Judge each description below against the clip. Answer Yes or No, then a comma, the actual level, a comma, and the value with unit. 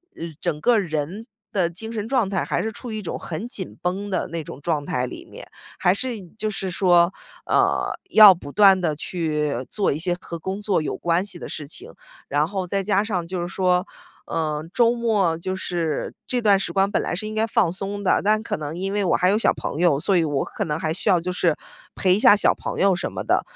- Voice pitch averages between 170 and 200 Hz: Yes, medium, 185 Hz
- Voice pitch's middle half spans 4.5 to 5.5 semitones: No, average, 3.6 semitones